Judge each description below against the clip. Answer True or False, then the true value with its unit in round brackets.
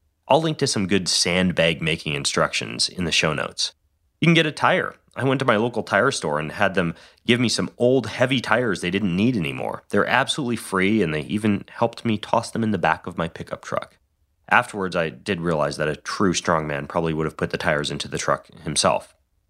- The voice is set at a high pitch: False (95 Hz)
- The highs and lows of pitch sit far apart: True (6.4 semitones)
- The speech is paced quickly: True (220 wpm)